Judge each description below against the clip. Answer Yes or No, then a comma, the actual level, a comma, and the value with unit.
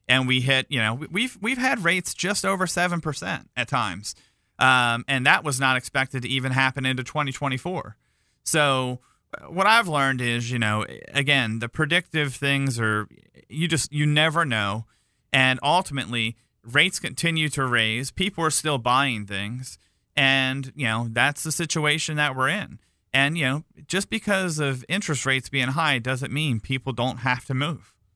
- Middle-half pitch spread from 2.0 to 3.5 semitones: No, average, 3.9 semitones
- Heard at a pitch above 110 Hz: Yes, low, 135 Hz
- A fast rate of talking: No, average, 170 wpm